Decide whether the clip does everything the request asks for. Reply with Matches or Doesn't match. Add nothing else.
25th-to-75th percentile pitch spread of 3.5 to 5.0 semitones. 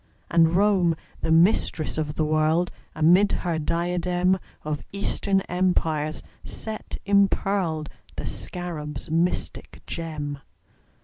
Doesn't match